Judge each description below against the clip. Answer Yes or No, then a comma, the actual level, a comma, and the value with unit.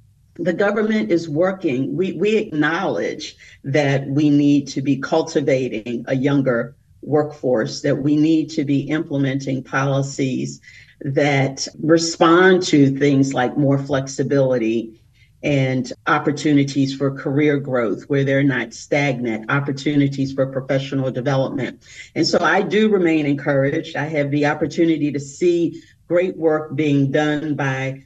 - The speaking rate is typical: No, slow, 130 wpm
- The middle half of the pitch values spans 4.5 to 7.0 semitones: No, narrow, 2.4 semitones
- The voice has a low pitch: No, medium, 145 Hz